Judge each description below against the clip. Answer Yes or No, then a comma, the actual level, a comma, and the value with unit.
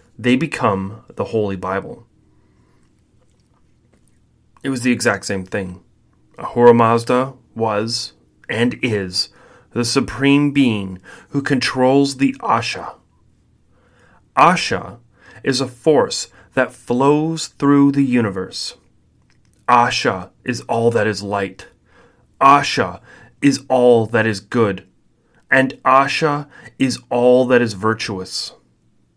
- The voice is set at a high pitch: No, low, 120 Hz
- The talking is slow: Yes, slow, 105 wpm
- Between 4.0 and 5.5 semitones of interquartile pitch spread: Yes, average, 4.8 semitones